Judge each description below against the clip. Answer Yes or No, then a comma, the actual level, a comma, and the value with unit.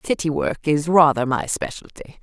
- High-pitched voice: No, low, 135 Hz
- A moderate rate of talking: Yes, average, 160 wpm